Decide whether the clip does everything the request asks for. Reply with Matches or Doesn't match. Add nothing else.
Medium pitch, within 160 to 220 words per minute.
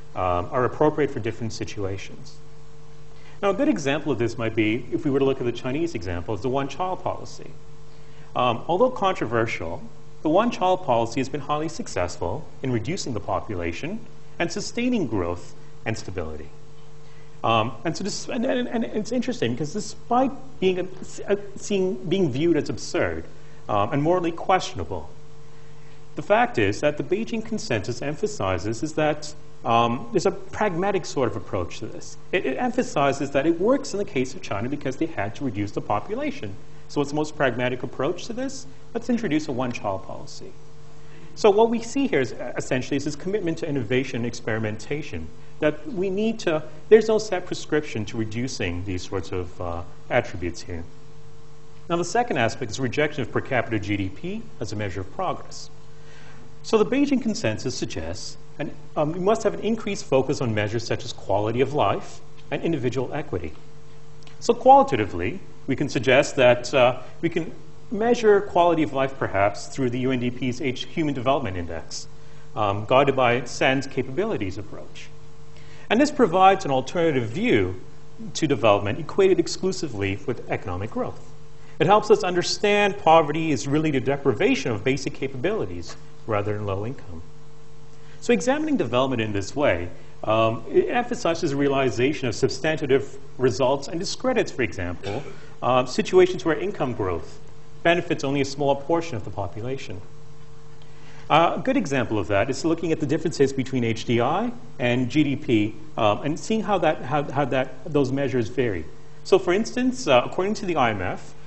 Matches